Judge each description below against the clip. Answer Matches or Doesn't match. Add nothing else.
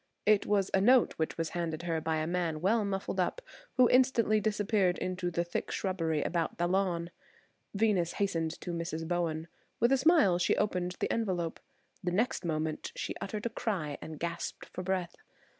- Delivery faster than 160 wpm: Matches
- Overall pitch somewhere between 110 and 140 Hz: Doesn't match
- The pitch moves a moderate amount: Matches